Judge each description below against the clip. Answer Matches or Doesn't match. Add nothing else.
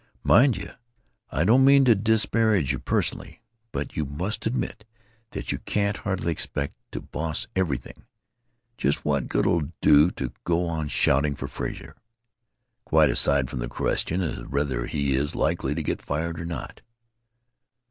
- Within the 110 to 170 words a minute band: Matches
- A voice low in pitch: Matches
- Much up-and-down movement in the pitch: Matches